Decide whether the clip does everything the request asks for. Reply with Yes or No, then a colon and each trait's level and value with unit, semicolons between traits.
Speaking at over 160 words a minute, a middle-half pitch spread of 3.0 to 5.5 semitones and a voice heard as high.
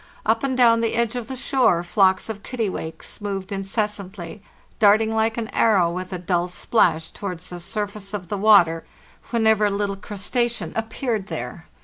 Yes: average, 175 wpm; average, 3.3 semitones; high, 205 Hz